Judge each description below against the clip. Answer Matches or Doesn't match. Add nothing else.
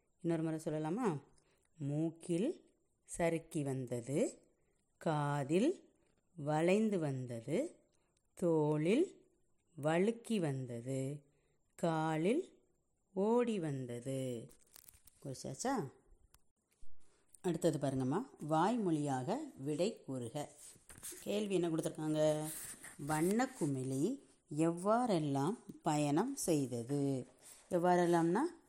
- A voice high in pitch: Doesn't match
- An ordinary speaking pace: Doesn't match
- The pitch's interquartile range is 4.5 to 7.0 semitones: Matches